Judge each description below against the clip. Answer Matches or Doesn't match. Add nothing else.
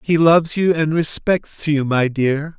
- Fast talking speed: Doesn't match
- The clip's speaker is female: Doesn't match